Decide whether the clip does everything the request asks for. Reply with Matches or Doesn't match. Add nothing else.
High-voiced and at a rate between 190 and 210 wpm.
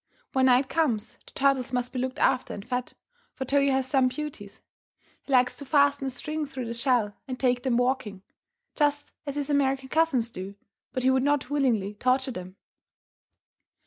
Doesn't match